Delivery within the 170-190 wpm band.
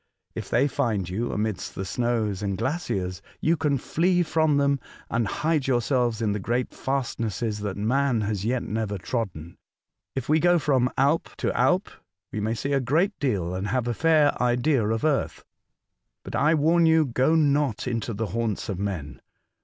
Yes: average, 175 wpm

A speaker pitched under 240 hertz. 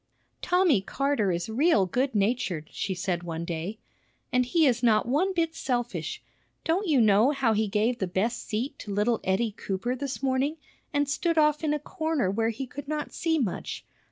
No: high, 245 Hz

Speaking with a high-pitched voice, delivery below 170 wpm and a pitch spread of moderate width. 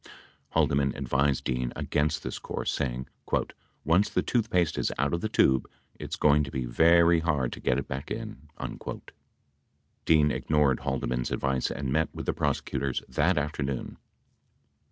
No: very low, 70 Hz; average, 155 wpm; average, 3.1 semitones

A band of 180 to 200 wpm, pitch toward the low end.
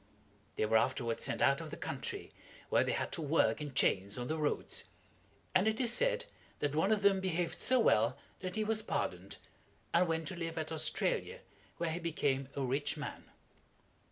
No: average, 190 wpm; medium, 160 Hz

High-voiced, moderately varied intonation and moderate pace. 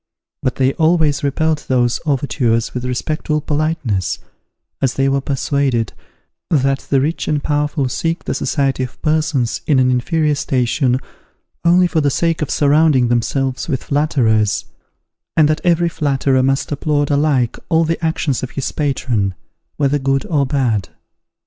No: medium, 140 Hz; average, 3.1 semitones; average, 150 wpm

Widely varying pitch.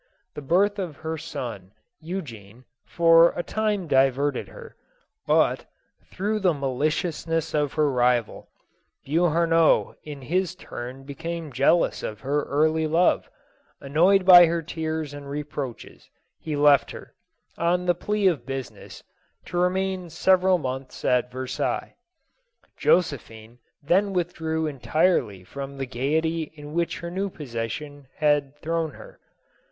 No: average, 4.1 semitones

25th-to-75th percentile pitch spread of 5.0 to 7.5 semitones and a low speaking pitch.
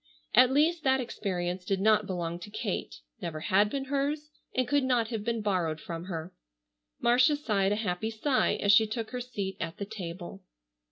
No: wide, 5.4 semitones; high, 210 Hz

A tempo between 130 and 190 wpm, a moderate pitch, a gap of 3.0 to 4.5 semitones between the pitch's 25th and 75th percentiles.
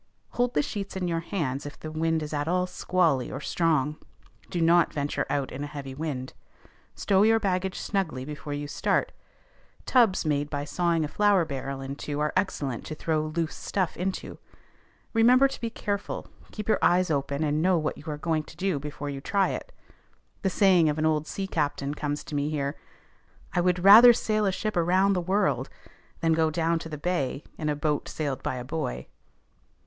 No: average, 200 wpm; medium, 160 Hz; average, 4.2 semitones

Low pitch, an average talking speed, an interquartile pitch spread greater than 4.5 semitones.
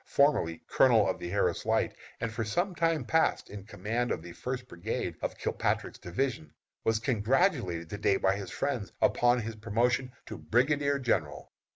Yes: low, 115 Hz; average, 170 wpm; average, 5.0 semitones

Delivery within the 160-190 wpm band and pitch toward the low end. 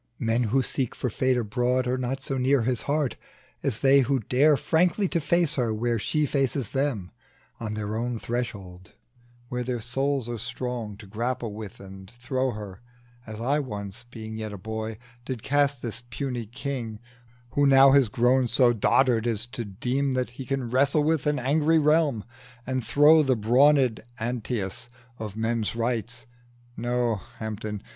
Yes: average, 165 wpm; low, 125 Hz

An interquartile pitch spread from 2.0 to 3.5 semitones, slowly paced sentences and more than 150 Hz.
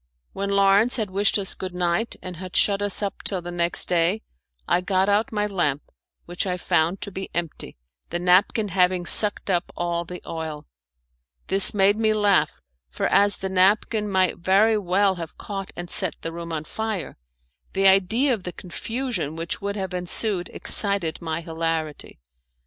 No: average, 2.8 semitones; average, 175 wpm; high, 190 Hz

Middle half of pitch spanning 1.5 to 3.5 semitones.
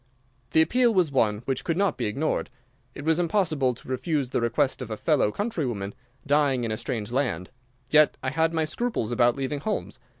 No: average, 5.0 semitones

